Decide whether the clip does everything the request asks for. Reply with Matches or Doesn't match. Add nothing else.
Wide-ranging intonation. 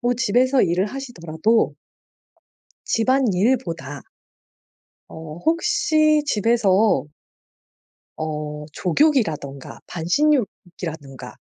Matches